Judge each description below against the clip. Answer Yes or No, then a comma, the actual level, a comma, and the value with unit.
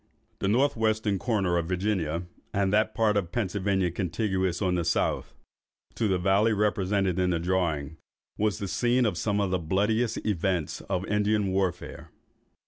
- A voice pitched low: Yes, very low, 95 Hz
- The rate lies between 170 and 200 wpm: No, average, 160 wpm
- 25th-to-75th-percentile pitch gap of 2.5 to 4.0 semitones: Yes, average, 2.8 semitones